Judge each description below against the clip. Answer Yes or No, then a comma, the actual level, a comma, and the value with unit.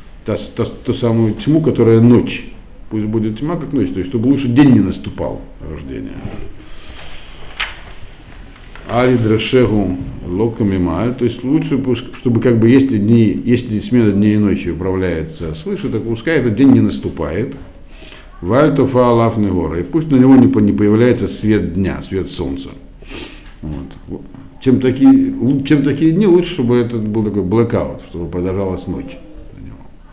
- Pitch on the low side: Yes, low, 115 Hz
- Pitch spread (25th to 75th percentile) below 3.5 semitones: No, average, 5.1 semitones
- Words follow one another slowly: No, average, 135 wpm